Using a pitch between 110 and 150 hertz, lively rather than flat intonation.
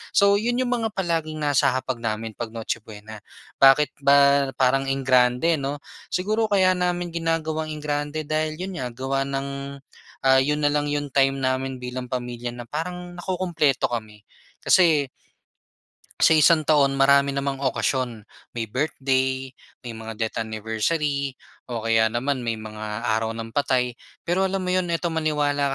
No: medium, 140 Hz; average, 4.4 semitones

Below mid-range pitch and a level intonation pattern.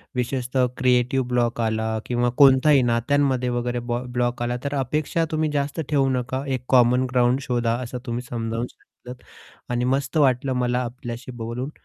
Yes: low, 125 Hz; narrow, 1.6 semitones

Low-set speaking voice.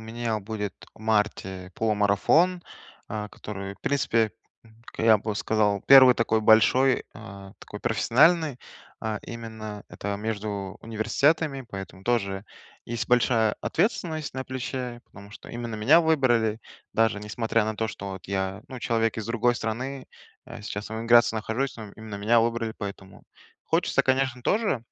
Yes: low, 110 Hz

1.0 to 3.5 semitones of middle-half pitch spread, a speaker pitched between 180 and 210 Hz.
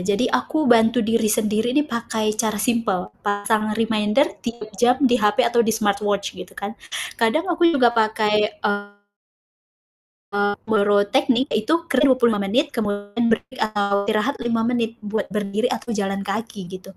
No: average, 2.7 semitones; high, 220 Hz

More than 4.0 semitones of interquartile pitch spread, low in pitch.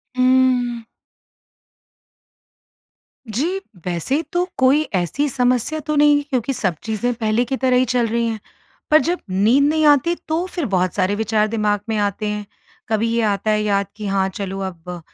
No: average, 4.5 semitones; high, 230 Hz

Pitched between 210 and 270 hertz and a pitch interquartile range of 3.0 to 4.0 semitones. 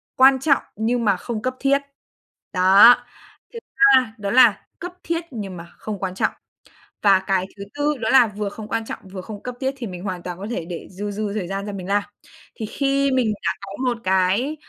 No: high, 215 Hz; average, 4.9 semitones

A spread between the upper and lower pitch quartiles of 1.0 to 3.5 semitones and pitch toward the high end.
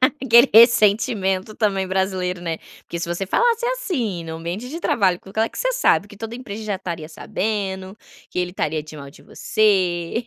No: average, 4.6 semitones; high, 195 Hz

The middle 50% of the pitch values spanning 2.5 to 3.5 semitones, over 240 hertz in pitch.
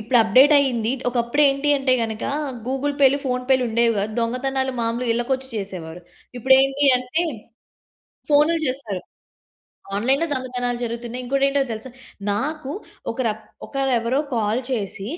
Yes: average, 2.8 semitones; very high, 255 Hz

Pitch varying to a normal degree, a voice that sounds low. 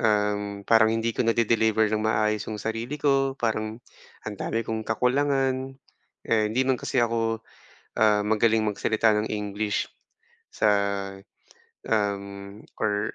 No: narrow, 1.6 semitones; low, 110 Hz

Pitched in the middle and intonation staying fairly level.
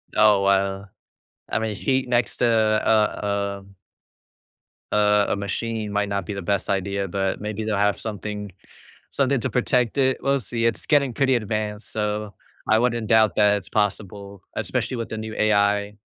No: low, 105 Hz; narrow, 2.0 semitones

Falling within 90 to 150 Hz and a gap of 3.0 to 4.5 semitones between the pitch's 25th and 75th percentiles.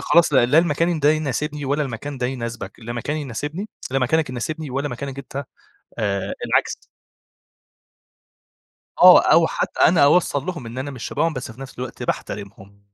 Yes: medium, 140 Hz; average, 3.9 semitones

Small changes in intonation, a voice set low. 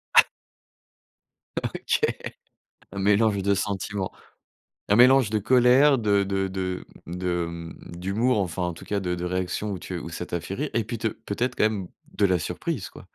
No: average, 3.3 semitones; low, 100 Hz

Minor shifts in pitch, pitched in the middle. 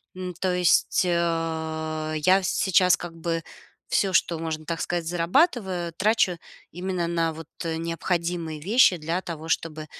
Yes: narrow, 1.9 semitones; medium, 170 Hz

